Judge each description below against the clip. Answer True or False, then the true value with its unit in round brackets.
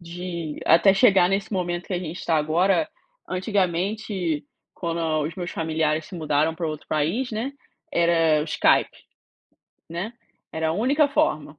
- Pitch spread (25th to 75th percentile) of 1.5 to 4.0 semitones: True (3.5 semitones)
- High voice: False (170 Hz)